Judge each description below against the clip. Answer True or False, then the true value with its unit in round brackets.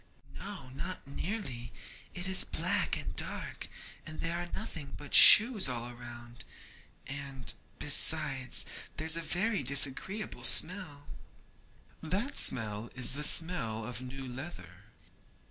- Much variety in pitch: True (6.3 semitones)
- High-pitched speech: False (140 Hz)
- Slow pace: True (120 wpm)